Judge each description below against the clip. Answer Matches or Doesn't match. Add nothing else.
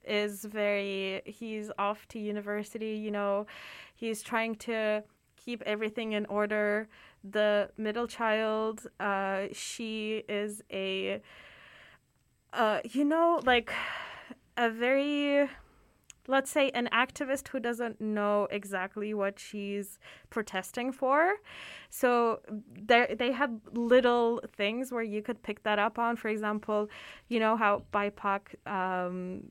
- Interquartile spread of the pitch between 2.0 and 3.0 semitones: Matches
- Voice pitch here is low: Doesn't match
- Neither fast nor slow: Doesn't match